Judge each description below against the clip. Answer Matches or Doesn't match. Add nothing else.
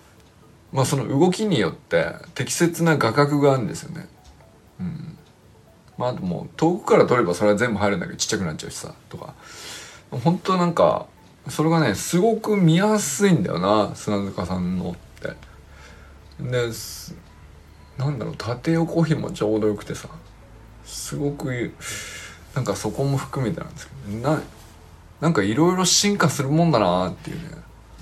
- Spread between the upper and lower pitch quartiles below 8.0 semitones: Doesn't match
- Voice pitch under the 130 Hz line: Doesn't match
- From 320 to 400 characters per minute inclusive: Doesn't match